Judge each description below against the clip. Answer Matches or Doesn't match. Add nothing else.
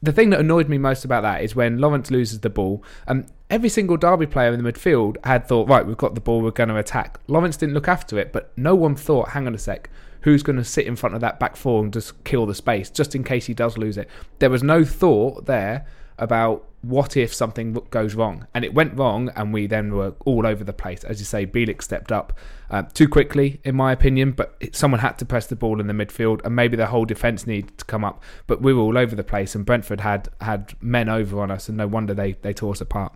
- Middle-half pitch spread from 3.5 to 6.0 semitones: Matches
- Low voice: Matches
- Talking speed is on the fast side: Matches